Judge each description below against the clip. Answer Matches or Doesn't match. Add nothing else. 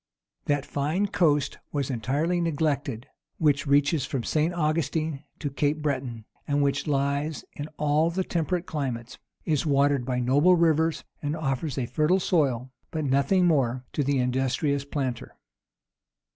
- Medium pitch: Matches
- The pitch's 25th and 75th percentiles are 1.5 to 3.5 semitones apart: Matches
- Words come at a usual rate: Matches